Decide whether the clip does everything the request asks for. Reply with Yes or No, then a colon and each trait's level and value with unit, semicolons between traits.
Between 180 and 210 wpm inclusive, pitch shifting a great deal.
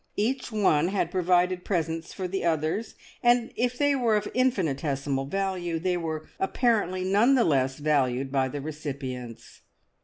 No: average, 150 wpm; wide, 6.1 semitones